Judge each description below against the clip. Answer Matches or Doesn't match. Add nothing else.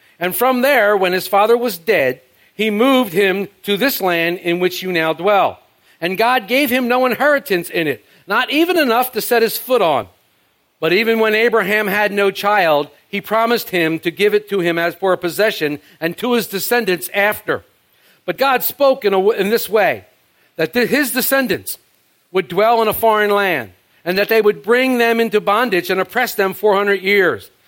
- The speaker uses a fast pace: Doesn't match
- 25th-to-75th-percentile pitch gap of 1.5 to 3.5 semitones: Doesn't match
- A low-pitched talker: Doesn't match